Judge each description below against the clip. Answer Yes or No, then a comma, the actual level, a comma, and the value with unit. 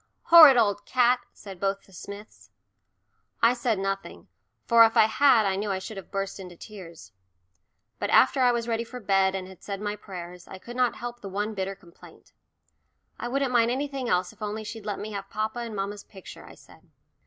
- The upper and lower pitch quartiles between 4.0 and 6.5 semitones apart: No, average, 3.5 semitones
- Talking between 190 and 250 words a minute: Yes, fast, 205 wpm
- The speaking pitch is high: Yes, high, 210 Hz